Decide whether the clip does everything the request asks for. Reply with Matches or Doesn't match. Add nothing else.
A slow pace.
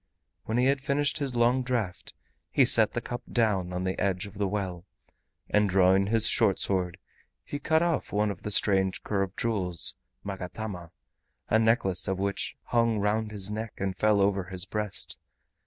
Doesn't match